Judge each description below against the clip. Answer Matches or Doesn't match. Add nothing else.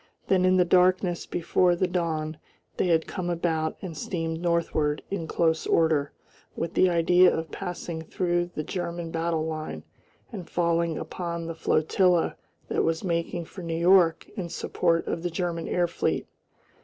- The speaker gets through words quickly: Doesn't match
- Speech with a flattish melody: Matches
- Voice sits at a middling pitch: Matches